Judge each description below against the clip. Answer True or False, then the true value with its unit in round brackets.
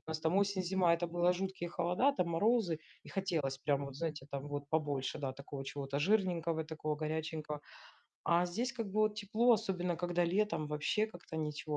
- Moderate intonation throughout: True (4.1 semitones)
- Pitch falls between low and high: True (170 Hz)